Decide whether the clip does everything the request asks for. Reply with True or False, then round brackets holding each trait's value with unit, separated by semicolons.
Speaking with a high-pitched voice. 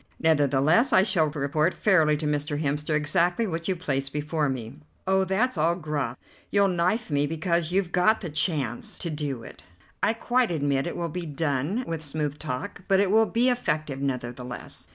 False (155 Hz)